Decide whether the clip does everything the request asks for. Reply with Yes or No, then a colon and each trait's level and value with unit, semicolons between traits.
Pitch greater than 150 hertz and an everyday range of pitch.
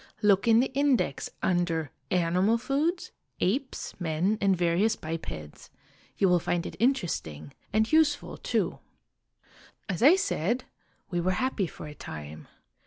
No: high, 190 Hz; wide, 7.0 semitones